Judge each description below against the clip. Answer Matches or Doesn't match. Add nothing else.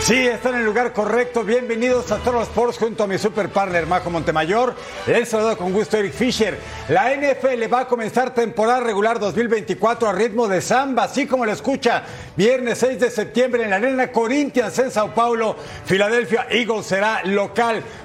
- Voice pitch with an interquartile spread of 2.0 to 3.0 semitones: Matches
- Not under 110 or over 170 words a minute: Doesn't match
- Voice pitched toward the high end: Matches